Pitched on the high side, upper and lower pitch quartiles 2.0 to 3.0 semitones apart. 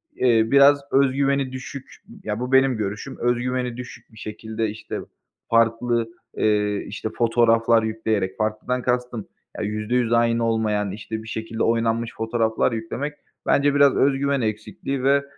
No: low, 115 Hz; narrow, 2.6 semitones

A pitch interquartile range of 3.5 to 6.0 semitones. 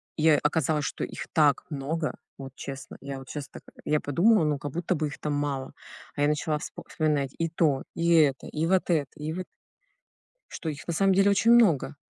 No: average, 2.7 semitones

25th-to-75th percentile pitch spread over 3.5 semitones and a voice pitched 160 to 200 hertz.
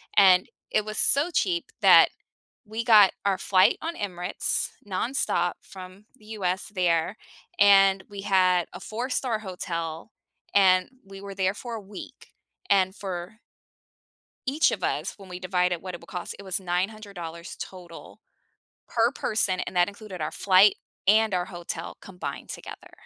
No: average, 2.8 semitones; high, 190 Hz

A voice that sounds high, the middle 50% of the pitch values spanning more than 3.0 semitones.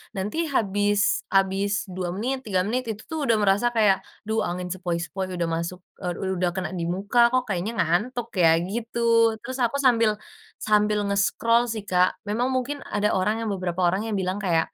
Yes: high, 200 Hz; average, 3.7 semitones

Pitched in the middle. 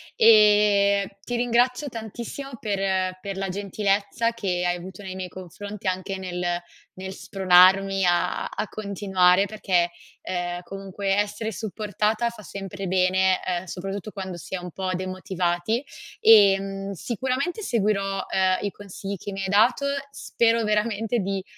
No: high, 195 Hz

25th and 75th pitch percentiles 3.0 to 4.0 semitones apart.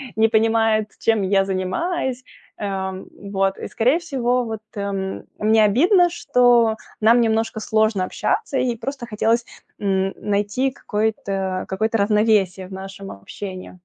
Yes: average, 3.3 semitones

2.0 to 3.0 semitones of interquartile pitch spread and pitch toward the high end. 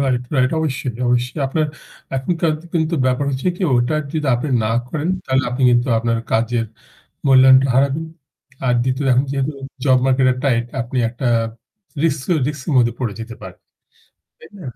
No: narrow, 2.6 semitones; low, 130 Hz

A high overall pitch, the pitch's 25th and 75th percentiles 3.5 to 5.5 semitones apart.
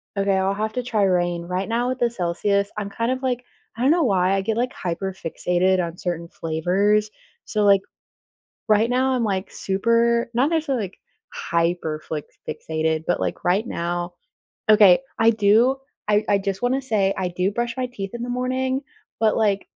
Yes: high, 200 Hz; average, 4.6 semitones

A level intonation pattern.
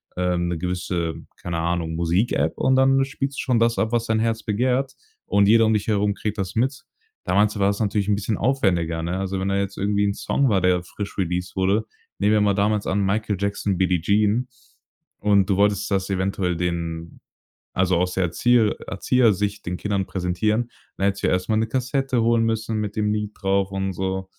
No: average, 3.0 semitones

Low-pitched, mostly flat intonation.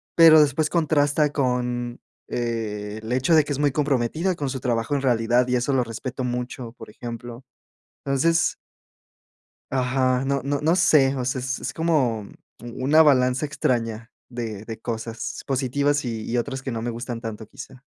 No: low, 125 Hz; average, 3.2 semitones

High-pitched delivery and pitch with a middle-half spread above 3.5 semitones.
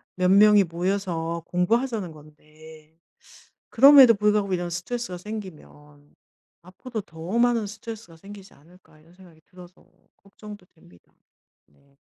No: medium, 180 Hz; average, 4.5 semitones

